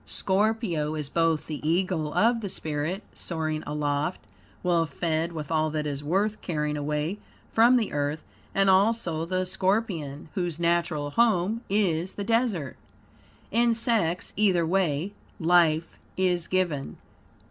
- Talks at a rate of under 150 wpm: Yes, slow, 135 wpm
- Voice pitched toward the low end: No, medium, 170 Hz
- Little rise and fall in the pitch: No, average, 4.2 semitones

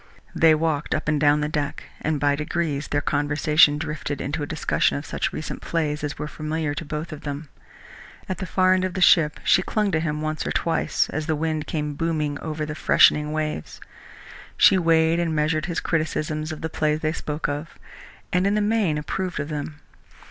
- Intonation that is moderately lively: No, narrow, 1.6 semitones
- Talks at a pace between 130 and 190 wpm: No, fast, 205 wpm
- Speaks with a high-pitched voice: No, medium, 155 Hz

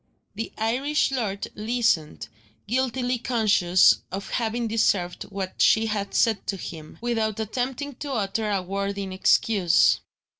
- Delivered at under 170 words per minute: Yes, slow, 135 wpm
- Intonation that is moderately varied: Yes, average, 3.5 semitones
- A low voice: No, high, 220 Hz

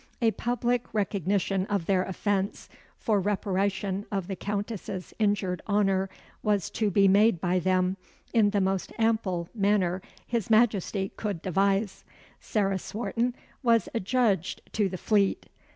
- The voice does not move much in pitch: Yes, narrow, 2.1 semitones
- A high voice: Yes, high, 200 Hz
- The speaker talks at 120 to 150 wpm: Yes, slow, 135 wpm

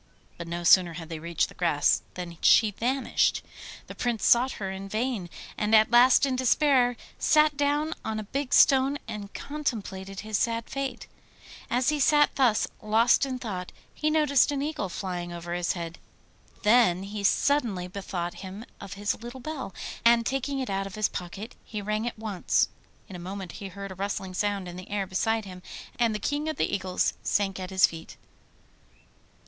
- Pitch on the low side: No, high, 210 Hz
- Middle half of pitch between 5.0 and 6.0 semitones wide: Yes, average, 5.3 semitones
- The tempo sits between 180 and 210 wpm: Yes, average, 185 wpm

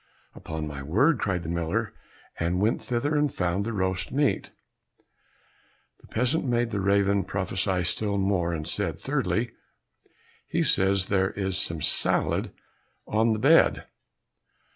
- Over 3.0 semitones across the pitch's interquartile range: Yes, average, 4.0 semitones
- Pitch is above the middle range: No, low, 100 Hz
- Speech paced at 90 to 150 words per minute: Yes, average, 140 wpm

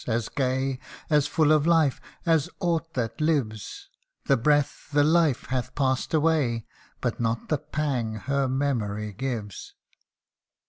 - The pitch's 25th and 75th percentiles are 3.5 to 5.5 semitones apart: Yes, average, 4.5 semitones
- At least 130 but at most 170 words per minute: Yes, slow, 135 wpm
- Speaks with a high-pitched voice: No, low, 135 Hz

